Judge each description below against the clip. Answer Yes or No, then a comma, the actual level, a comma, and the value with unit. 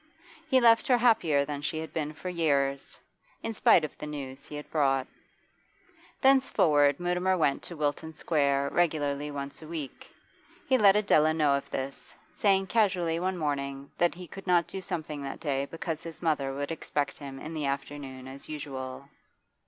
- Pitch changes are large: No, average, 3.8 semitones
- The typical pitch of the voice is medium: Yes, medium, 150 Hz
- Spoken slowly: No, average, 175 wpm